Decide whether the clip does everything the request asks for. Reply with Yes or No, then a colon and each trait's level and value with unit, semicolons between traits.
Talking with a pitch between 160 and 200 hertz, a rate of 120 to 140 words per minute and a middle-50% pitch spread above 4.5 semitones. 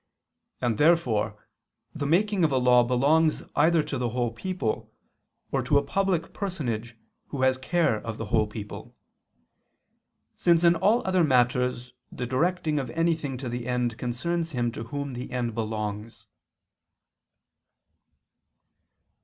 No: low, 130 Hz; slow, 135 wpm; wide, 5.6 semitones